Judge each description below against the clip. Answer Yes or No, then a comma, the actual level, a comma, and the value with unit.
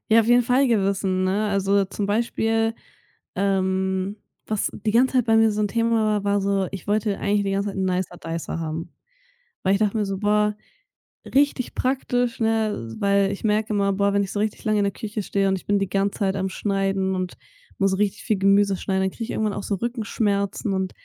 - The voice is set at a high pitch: Yes, high, 200 Hz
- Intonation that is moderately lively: No, narrow, 2.0 semitones